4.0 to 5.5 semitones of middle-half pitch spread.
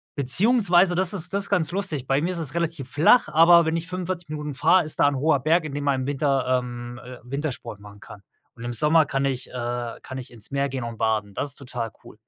Yes: average, 5.1 semitones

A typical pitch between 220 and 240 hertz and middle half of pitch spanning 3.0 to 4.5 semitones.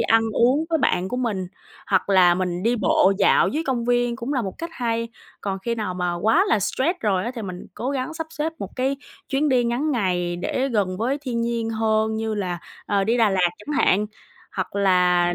No: high, 225 Hz; average, 5.1 semitones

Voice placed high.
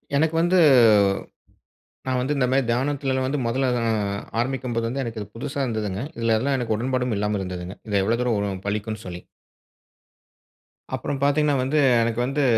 No: low, 120 Hz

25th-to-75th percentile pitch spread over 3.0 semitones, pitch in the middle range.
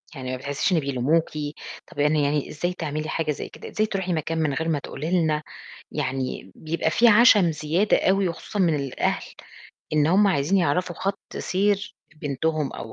Yes: average, 4.0 semitones; medium, 160 Hz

